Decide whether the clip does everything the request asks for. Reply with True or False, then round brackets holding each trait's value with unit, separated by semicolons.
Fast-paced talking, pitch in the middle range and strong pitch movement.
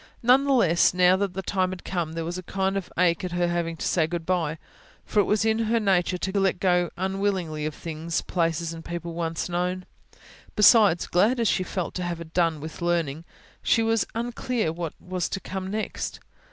False (210 wpm; 180 Hz; 2.7 semitones)